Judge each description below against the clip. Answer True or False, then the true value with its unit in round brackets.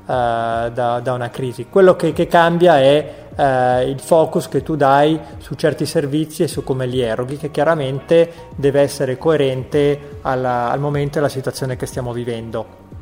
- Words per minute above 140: True (170 wpm)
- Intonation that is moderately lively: True (3.4 semitones)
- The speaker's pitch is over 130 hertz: True (140 Hz)